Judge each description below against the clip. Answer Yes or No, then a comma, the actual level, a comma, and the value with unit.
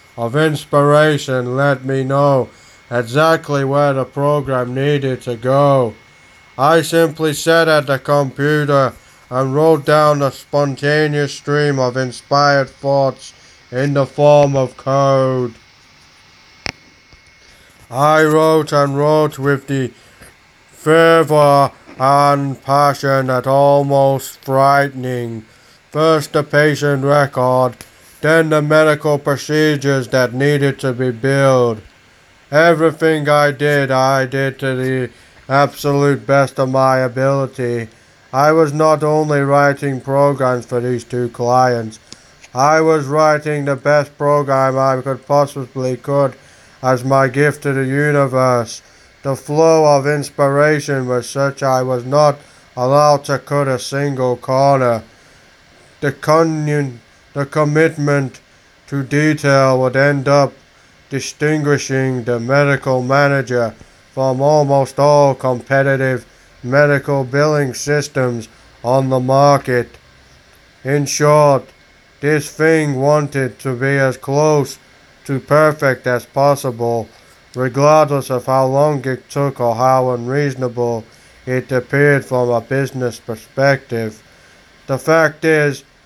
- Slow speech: Yes, slow, 115 wpm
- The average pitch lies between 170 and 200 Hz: No, medium, 140 Hz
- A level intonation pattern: Yes, narrow, 2.2 semitones